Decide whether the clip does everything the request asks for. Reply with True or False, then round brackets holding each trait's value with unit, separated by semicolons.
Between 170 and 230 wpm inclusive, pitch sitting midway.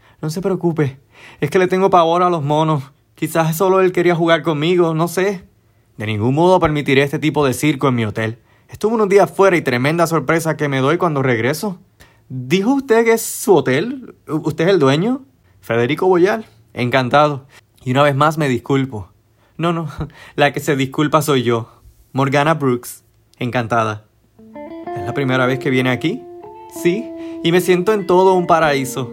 True (180 wpm; 150 Hz)